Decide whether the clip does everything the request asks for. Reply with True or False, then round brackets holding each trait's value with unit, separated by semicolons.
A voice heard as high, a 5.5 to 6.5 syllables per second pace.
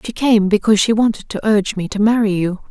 True (210 Hz; 6.4 syllables/s)